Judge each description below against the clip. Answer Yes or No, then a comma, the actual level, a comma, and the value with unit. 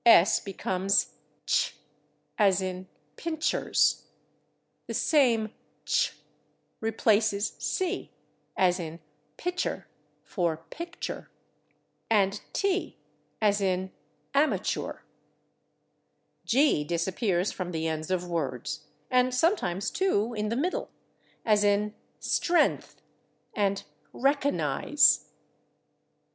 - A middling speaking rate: No, slow, 90 wpm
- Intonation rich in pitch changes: Yes, wide, 6.0 semitones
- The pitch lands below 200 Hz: No, high, 205 Hz